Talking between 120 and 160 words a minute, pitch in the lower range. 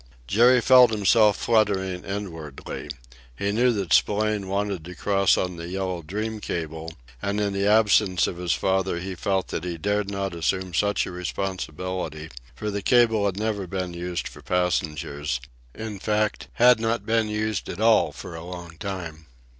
No: average, 170 wpm; very low, 95 Hz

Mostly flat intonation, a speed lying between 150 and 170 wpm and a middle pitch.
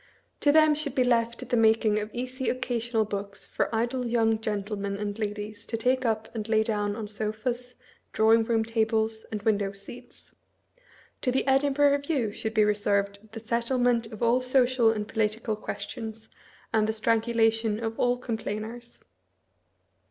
No: narrow, 2.3 semitones; average, 155 wpm; high, 225 Hz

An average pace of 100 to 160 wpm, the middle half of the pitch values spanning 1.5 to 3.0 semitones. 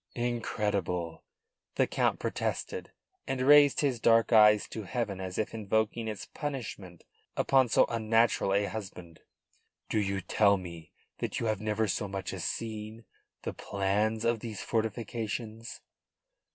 Yes: average, 140 wpm; narrow, 2.6 semitones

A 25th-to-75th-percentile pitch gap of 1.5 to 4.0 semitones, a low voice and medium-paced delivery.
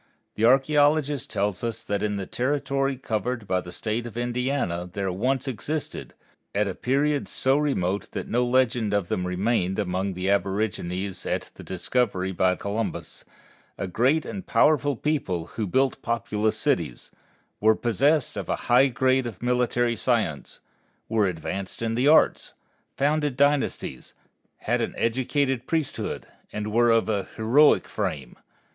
No: average, 5.1 semitones; low, 115 Hz; average, 150 wpm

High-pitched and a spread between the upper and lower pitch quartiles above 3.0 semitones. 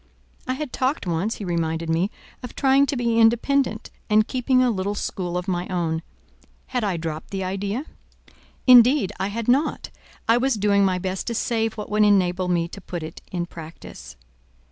Yes: high, 205 Hz; average, 5.2 semitones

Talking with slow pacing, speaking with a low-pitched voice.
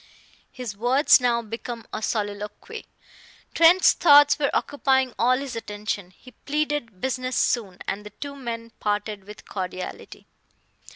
No: slow, 130 wpm; high, 235 Hz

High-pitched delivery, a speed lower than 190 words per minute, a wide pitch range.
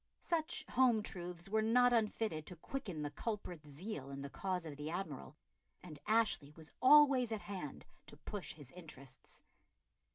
No: medium, 180 Hz; average, 160 wpm; wide, 6.9 semitones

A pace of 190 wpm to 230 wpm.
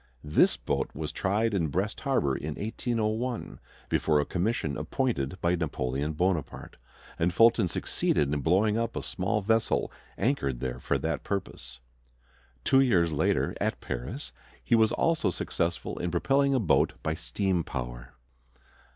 No: average, 145 wpm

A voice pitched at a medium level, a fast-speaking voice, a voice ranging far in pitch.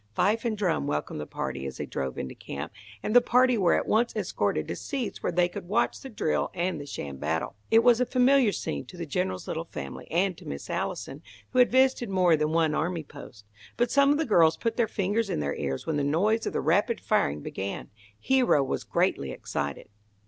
Yes: medium, 180 Hz; fast, 220 wpm; wide, 8.8 semitones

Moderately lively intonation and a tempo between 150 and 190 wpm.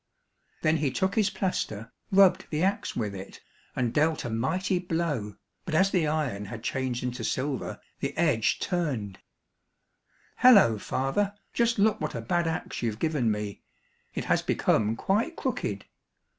No: wide, 8.4 semitones; average, 155 wpm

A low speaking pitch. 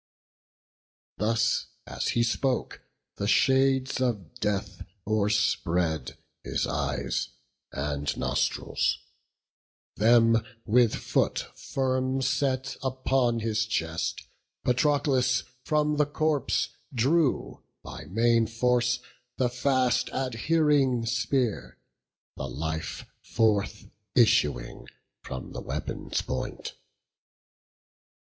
Yes: low, 120 Hz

